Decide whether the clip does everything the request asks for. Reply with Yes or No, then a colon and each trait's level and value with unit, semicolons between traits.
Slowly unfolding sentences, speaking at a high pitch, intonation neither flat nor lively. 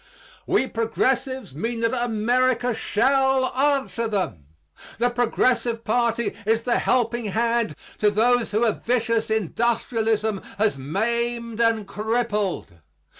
No: slow, 115 wpm; high, 230 Hz; narrow, 1.9 semitones